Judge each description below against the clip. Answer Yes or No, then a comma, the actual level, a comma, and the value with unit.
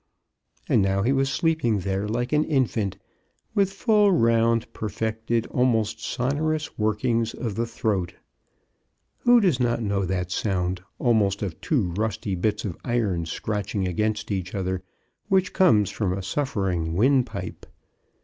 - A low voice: Yes, low, 110 Hz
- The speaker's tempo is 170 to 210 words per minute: No, average, 145 wpm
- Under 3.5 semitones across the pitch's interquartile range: No, average, 4.5 semitones